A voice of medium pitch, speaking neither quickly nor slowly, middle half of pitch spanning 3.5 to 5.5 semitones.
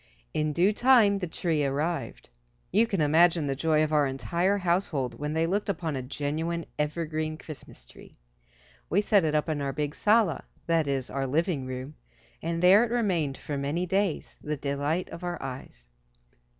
Yes: medium, 160 Hz; average, 175 wpm; average, 3.8 semitones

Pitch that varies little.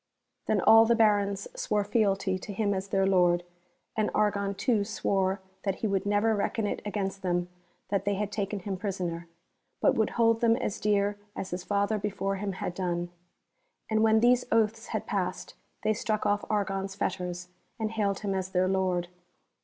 Yes: narrow, 1.9 semitones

